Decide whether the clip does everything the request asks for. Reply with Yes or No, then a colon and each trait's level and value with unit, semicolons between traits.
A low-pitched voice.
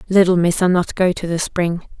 No: medium, 175 Hz